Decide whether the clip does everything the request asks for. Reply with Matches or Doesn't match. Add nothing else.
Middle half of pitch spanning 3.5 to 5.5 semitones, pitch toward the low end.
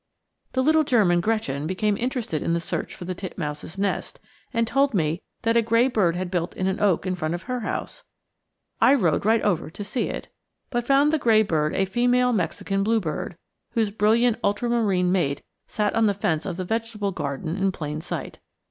Doesn't match